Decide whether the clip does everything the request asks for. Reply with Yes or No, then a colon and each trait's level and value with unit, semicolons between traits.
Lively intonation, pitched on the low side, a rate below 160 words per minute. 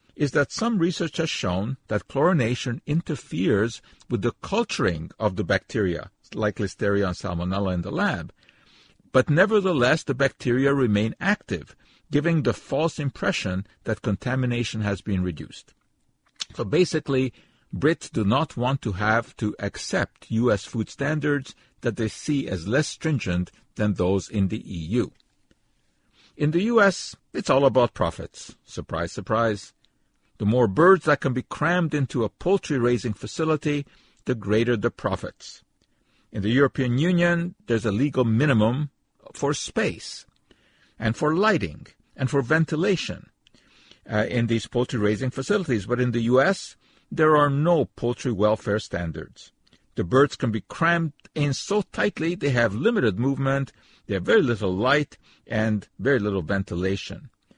Yes: wide, 5.7 semitones; low, 120 Hz; average, 145 wpm